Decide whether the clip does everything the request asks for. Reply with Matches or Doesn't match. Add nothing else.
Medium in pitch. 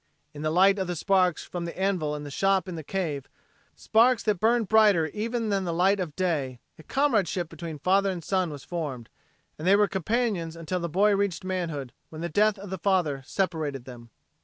Matches